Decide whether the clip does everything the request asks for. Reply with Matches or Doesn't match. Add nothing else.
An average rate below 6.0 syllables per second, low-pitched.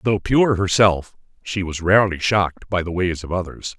Matches